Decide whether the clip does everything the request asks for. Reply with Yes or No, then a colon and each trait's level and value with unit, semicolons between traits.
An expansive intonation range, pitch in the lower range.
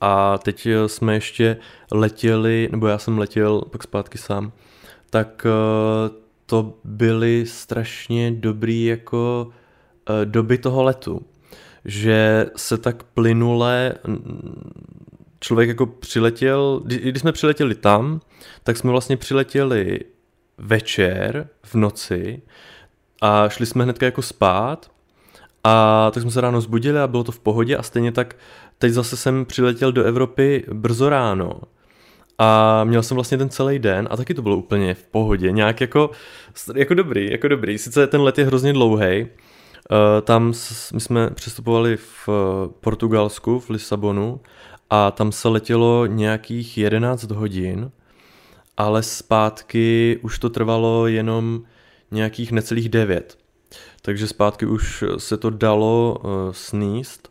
No: narrow, 2.4 semitones; low, 115 Hz